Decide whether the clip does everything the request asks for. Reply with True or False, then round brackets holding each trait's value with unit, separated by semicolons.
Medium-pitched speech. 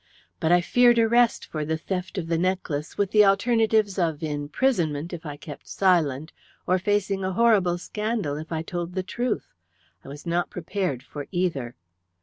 True (180 Hz)